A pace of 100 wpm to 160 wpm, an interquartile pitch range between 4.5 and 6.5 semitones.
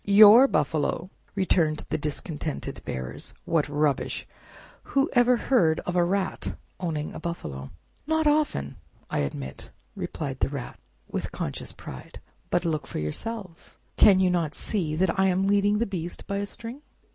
Yes: average, 150 wpm; average, 5.2 semitones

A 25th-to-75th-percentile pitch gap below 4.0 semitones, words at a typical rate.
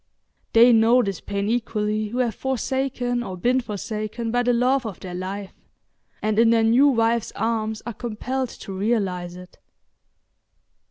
Yes: average, 2.9 semitones; average, 155 wpm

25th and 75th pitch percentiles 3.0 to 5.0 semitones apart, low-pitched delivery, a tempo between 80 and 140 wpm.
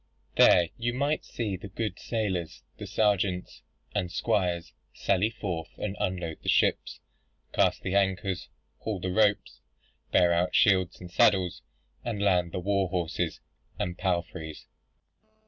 No: narrow, 2.6 semitones; very low, 95 Hz; slow, 135 wpm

